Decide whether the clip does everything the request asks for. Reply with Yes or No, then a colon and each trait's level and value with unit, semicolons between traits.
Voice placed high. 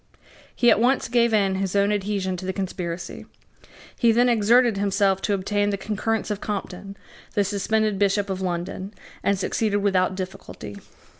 Yes: high, 200 Hz